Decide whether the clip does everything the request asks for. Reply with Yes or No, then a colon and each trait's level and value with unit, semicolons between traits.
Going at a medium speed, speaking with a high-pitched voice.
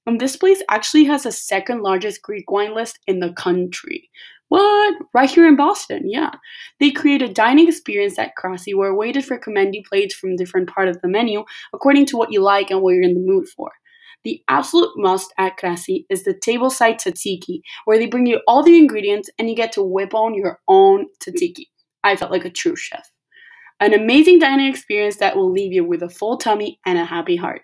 No: fast, 215 wpm; high, 225 Hz